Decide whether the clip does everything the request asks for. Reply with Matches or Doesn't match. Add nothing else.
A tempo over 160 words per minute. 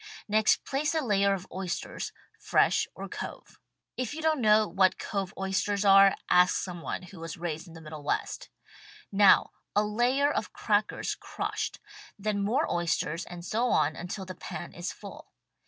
Matches